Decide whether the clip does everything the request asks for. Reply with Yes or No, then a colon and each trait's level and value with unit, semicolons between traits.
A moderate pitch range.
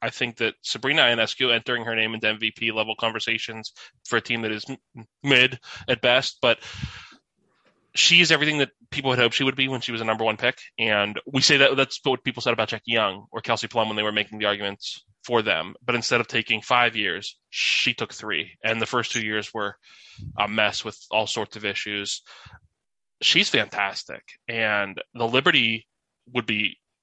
No: narrow, 2.3 semitones